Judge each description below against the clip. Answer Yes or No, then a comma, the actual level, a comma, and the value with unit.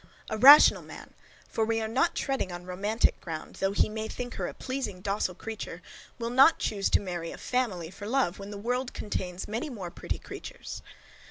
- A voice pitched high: Yes, high, 215 Hz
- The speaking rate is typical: Yes, average, 195 wpm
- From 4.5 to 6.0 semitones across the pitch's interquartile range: Yes, average, 4.8 semitones